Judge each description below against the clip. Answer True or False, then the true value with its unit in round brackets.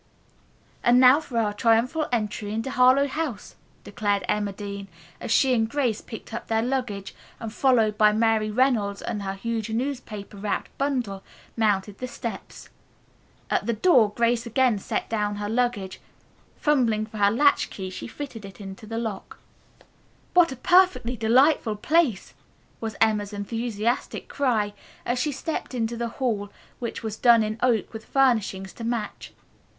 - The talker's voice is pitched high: True (225 Hz)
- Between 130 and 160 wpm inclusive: True (155 wpm)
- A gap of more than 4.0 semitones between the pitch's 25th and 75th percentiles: False (3.2 semitones)